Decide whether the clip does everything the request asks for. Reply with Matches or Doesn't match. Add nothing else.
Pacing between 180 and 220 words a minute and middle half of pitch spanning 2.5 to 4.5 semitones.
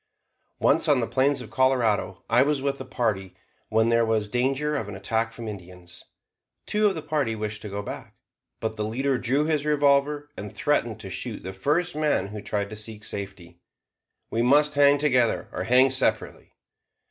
Doesn't match